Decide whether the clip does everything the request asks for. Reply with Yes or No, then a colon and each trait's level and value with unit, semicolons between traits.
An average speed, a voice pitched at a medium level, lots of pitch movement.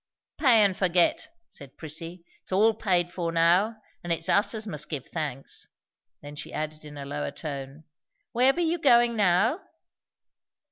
Yes: average, 160 wpm; medium, 175 Hz; wide, 6.2 semitones